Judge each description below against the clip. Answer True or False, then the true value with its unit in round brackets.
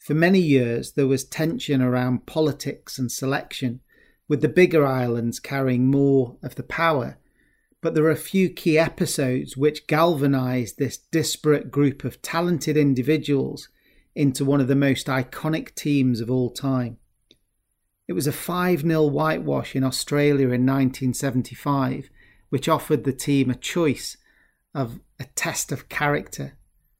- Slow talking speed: False (145 wpm)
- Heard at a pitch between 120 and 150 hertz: True (140 Hz)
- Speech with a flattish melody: False (3.2 semitones)